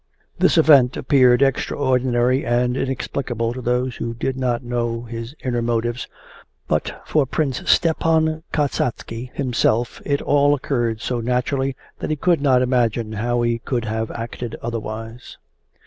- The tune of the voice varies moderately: No, narrow, 2.3 semitones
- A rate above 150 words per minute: No, average, 140 wpm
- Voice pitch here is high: No, low, 125 Hz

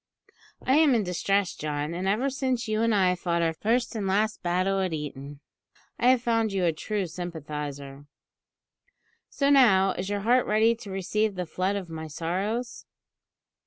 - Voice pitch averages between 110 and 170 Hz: No, high, 195 Hz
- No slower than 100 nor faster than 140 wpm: No, average, 170 wpm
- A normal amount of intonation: Yes, average, 4.9 semitones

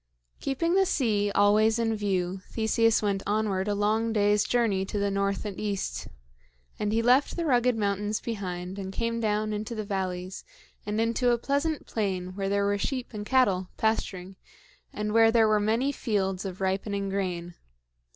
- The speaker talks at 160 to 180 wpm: Yes, average, 170 wpm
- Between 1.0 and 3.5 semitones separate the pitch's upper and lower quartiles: Yes, narrow, 2.6 semitones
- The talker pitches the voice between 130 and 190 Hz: No, high, 210 Hz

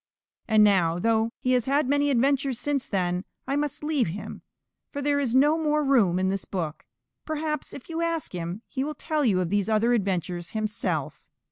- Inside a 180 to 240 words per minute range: Yes, average, 195 wpm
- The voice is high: Yes, high, 245 Hz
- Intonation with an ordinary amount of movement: No, wide, 6.9 semitones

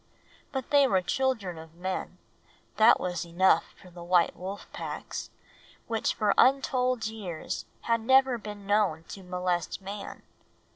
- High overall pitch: Yes, high, 200 Hz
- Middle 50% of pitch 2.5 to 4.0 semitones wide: No, average, 4.5 semitones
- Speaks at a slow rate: No, average, 145 wpm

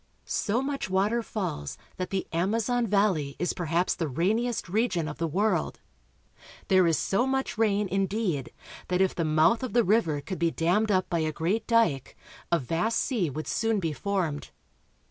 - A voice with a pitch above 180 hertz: Yes, high, 190 Hz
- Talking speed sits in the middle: Yes, average, 175 wpm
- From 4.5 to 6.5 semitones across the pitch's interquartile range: Yes, average, 5.0 semitones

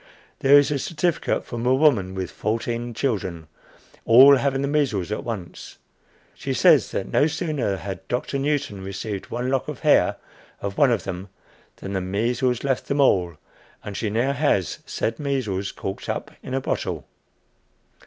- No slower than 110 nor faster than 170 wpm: Yes, average, 165 wpm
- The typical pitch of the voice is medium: No, low, 120 Hz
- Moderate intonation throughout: No, wide, 6.1 semitones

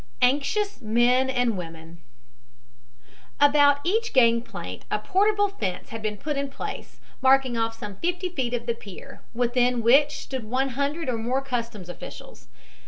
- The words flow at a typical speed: Yes, average, 150 wpm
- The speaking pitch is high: Yes, very high, 250 Hz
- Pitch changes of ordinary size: Yes, average, 4.0 semitones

